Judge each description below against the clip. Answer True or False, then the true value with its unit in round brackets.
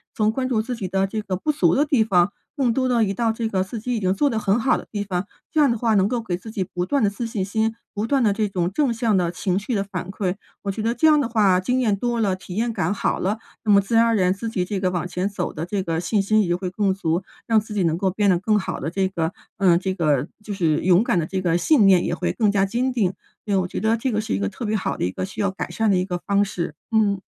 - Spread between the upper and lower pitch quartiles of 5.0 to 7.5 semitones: False (3.3 semitones)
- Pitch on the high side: True (200 Hz)